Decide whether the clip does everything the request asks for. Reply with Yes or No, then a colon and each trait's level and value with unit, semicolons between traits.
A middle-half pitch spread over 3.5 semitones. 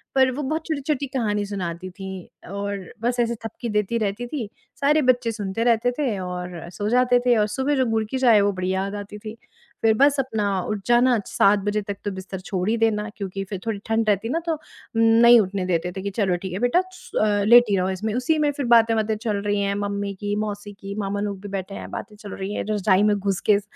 No: average, 3.2 semitones